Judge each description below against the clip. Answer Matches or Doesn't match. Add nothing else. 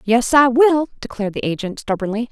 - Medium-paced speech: Matches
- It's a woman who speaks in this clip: Matches